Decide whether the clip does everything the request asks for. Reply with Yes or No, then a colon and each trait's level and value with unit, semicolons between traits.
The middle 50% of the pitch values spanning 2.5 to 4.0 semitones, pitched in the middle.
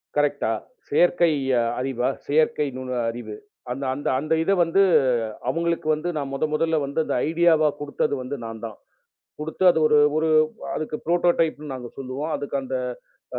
Yes: average, 3.5 semitones; medium, 150 Hz